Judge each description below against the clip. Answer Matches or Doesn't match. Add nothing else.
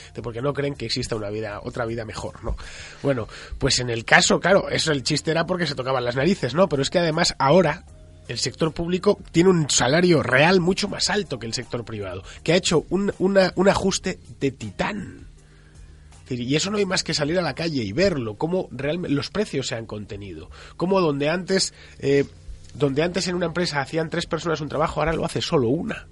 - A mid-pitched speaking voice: Matches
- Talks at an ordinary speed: Doesn't match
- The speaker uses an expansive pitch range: Matches